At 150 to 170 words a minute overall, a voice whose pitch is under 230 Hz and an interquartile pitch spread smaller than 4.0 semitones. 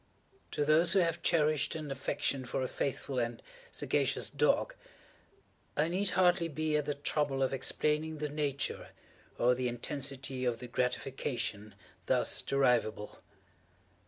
No: slow, 135 wpm; medium, 140 Hz; average, 3.4 semitones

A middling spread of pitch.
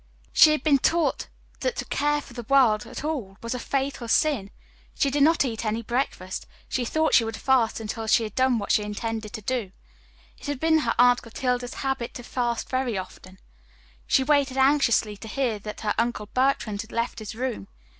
Yes: average, 3.8 semitones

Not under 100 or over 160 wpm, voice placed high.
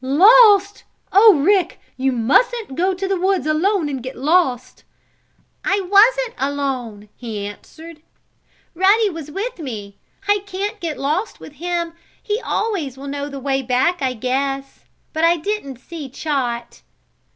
Yes: average, 145 wpm; very high, 315 Hz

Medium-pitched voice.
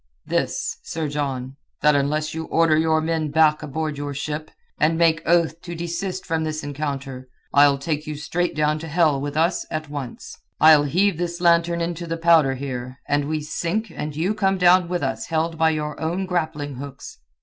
Yes: medium, 155 Hz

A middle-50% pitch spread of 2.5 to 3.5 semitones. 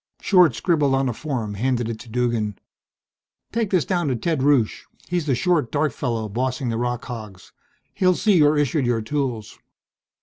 No: average, 4.9 semitones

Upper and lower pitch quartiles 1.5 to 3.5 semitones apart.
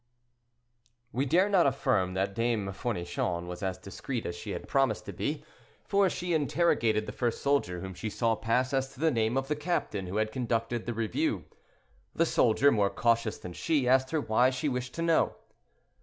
No: average, 4.7 semitones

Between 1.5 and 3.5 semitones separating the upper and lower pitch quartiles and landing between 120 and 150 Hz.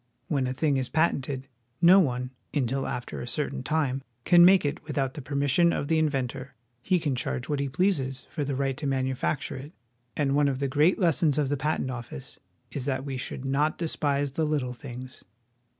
Yes: narrow, 2.6 semitones; medium, 140 Hz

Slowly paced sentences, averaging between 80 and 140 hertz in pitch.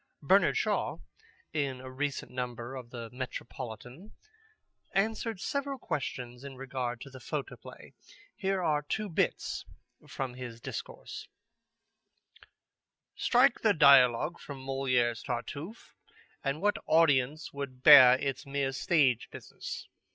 Yes: slow, 115 wpm; low, 135 Hz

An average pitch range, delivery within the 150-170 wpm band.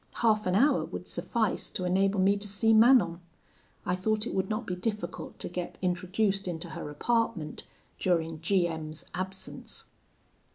Yes: average, 3.4 semitones; average, 165 wpm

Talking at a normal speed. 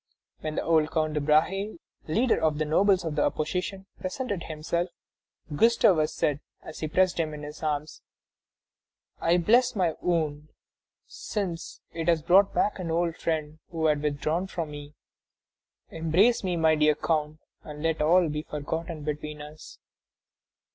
Yes: average, 155 wpm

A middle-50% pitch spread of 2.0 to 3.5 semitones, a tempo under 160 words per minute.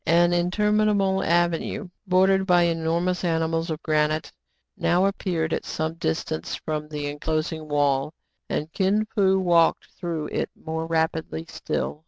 Yes: average, 2.7 semitones; slow, 135 wpm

